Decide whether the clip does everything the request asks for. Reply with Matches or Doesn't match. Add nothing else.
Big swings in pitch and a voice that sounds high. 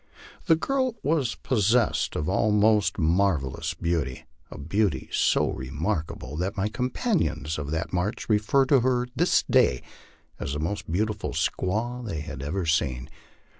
Doesn't match